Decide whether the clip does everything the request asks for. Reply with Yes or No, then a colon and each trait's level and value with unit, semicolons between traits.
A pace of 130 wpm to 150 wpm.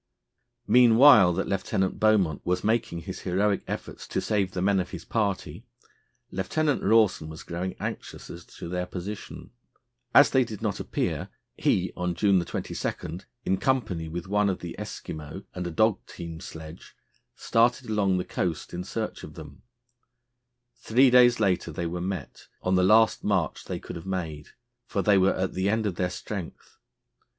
No: average, 170 wpm